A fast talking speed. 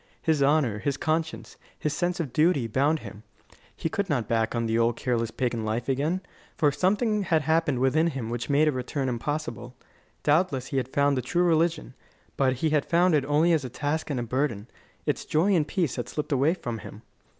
Yes: fast, 210 wpm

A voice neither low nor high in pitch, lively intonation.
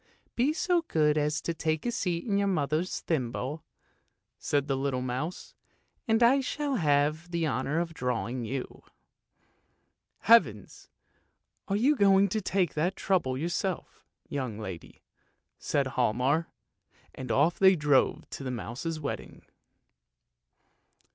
Yes: medium, 155 Hz; wide, 6.3 semitones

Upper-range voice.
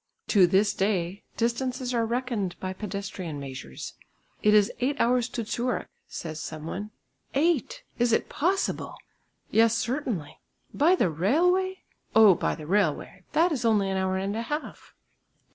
Yes: high, 215 Hz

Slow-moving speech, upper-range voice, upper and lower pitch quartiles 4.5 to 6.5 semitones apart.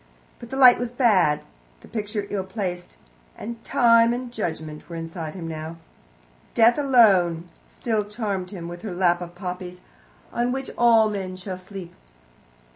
No: average, 155 wpm; high, 195 Hz; average, 4.8 semitones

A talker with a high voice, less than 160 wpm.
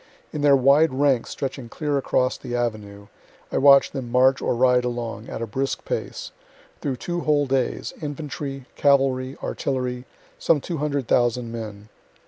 No: low, 130 Hz; average, 145 wpm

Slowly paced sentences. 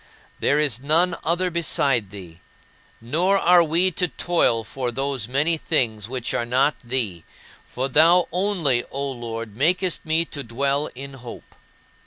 No: average, 150 wpm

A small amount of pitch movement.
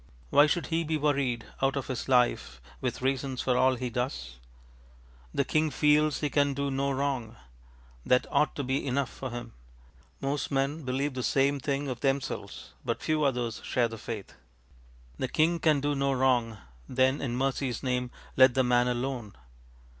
Yes: narrow, 2.2 semitones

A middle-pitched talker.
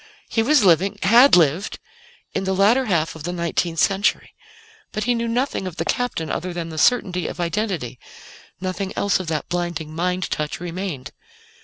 Yes: medium, 180 Hz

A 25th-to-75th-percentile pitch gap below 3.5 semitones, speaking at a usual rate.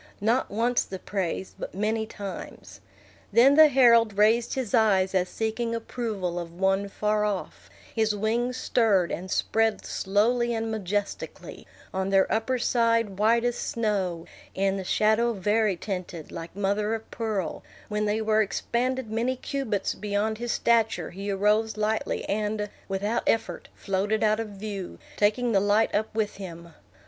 Yes: narrow, 2.6 semitones; average, 155 wpm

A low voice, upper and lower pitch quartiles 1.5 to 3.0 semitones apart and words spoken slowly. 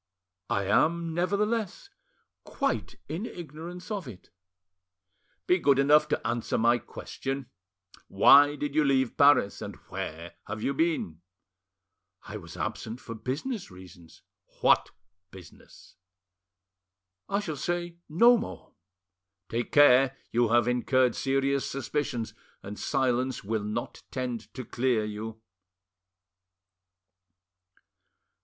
No: low, 130 Hz; wide, 5.6 semitones; slow, 110 wpm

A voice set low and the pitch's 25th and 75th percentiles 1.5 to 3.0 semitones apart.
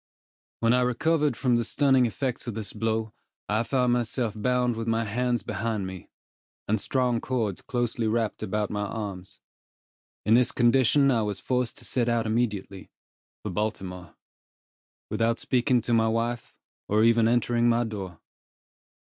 Yes: low, 115 Hz; narrow, 2.4 semitones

